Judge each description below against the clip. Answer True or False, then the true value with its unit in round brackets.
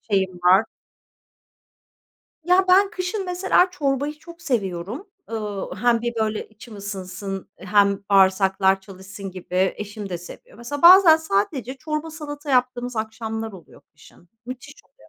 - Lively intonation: True (7.6 semitones)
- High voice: True (225 Hz)